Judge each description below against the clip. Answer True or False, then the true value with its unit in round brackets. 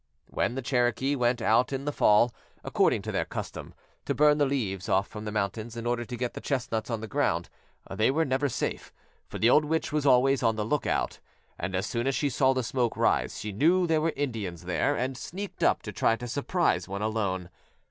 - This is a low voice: True (120 Hz)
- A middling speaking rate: False (220 wpm)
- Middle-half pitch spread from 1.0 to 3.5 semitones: False (4.3 semitones)